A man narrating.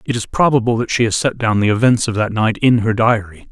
Yes: male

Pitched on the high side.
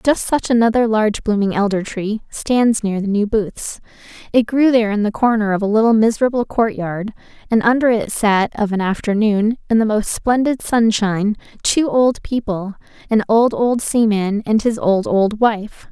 Yes: high, 220 Hz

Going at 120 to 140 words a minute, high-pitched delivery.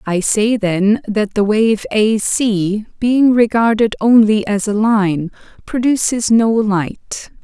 Yes: slow, 135 wpm; high, 215 Hz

